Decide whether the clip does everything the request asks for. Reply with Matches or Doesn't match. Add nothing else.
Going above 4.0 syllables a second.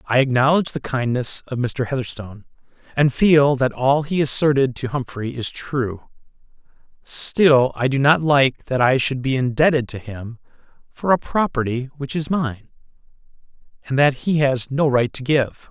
Matches